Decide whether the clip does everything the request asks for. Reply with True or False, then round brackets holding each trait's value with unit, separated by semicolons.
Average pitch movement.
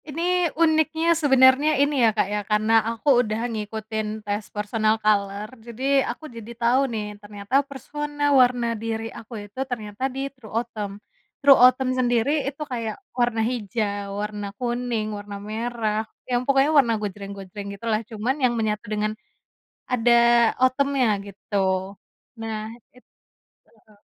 True (3.6 semitones)